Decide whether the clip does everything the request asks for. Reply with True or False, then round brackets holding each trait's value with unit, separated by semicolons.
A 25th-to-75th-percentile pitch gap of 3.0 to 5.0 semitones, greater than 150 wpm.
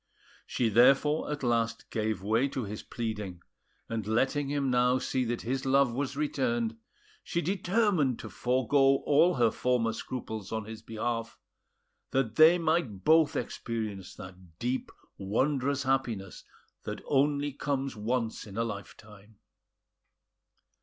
False (4.3 semitones; 135 wpm)